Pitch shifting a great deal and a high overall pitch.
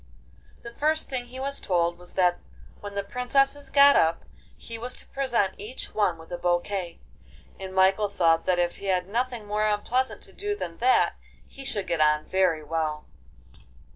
Yes: wide, 6.2 semitones; high, 200 Hz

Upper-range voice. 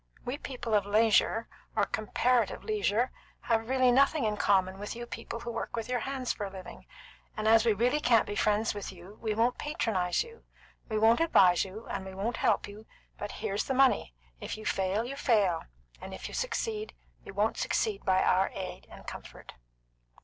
Yes: high, 220 Hz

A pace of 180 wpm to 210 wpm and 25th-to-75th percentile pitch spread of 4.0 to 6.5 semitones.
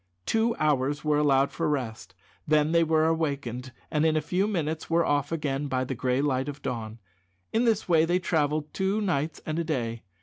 No: average, 200 wpm; average, 3.3 semitones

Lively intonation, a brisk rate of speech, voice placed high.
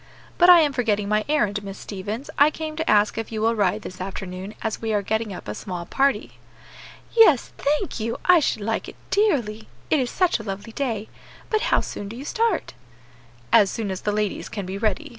Yes: wide, 5.9 semitones; fast, 215 wpm; high, 220 Hz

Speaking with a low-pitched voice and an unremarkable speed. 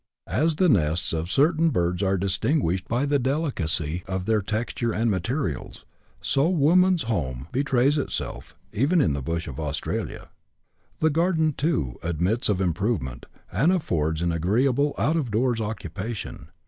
Yes: low, 110 Hz; average, 150 wpm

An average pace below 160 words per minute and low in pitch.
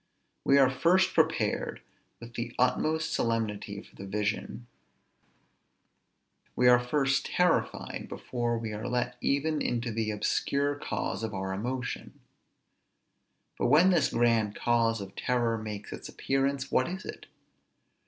Yes: slow, 135 wpm; low, 120 Hz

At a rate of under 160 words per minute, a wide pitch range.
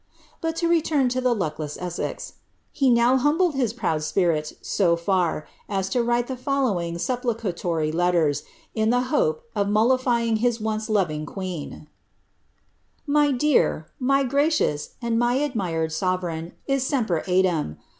Yes: average, 145 wpm; wide, 6.9 semitones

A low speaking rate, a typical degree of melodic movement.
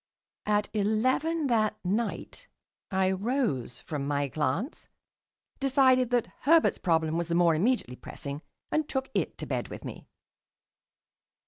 No: slow, 130 wpm; wide, 8.1 semitones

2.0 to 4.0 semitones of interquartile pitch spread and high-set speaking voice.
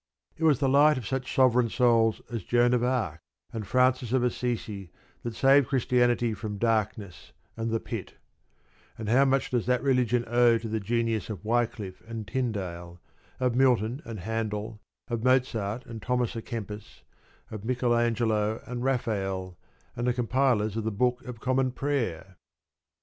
No: narrow, 2.6 semitones; low, 115 Hz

